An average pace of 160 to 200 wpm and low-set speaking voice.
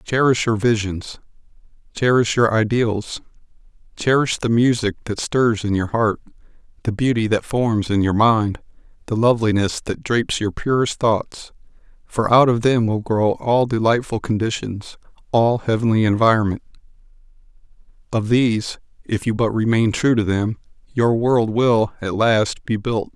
No: average, 145 wpm; low, 115 Hz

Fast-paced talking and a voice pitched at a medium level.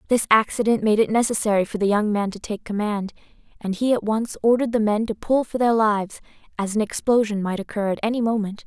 No: fast, 220 wpm; high, 215 Hz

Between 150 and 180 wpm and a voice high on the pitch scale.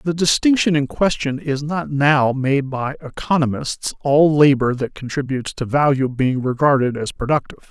No: average, 155 wpm; medium, 140 Hz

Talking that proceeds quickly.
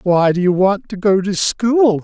Yes: fast, 235 wpm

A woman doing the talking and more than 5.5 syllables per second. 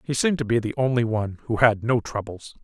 No: male; 6.5 syllables/s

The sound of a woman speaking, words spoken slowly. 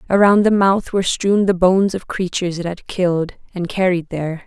No: female; average, 200 wpm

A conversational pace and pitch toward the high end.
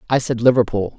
No: average, 185 wpm; low, 120 Hz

